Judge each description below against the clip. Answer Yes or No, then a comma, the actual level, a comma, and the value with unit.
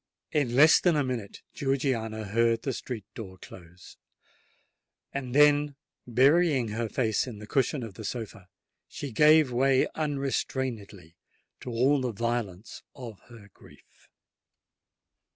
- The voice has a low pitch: Yes, low, 120 Hz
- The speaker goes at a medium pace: No, slow, 130 wpm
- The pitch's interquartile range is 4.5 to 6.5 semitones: No, average, 4.0 semitones